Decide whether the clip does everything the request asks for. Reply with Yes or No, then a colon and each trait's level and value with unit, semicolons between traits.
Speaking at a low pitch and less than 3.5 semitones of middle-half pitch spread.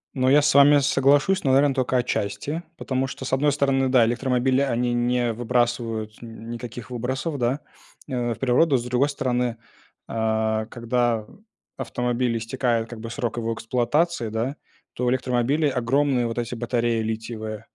Yes: low, 125 Hz; narrow, 2.5 semitones